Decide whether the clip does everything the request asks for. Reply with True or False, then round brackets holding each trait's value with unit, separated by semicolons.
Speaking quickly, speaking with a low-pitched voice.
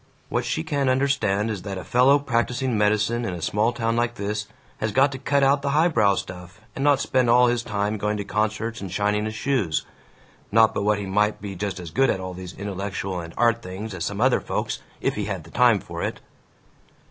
True (225 wpm; 110 Hz)